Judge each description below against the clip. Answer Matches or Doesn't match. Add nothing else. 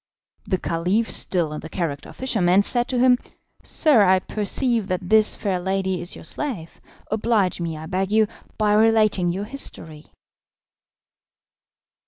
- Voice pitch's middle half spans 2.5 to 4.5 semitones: Matches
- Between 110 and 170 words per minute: Matches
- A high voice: Matches